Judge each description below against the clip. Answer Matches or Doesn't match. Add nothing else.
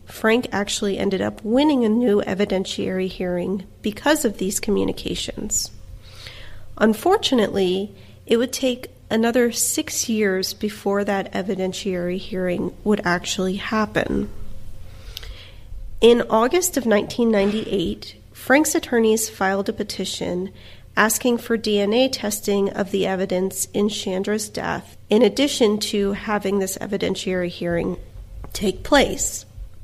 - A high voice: Matches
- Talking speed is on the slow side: Matches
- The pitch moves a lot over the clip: Doesn't match